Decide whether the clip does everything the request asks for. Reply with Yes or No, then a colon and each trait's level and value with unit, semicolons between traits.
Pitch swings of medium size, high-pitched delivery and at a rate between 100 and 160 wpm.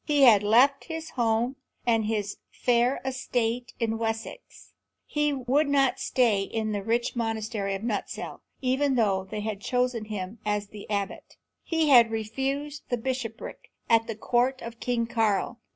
Yes: average, 3.1 semitones; high, 230 Hz; average, 155 wpm